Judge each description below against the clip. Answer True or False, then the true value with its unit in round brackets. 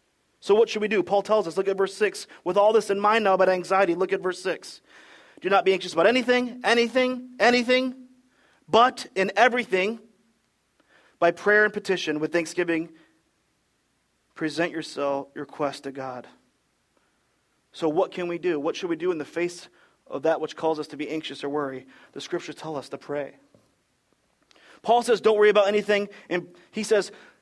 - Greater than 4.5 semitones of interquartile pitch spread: True (4.9 semitones)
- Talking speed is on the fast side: False (185 wpm)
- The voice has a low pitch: False (195 Hz)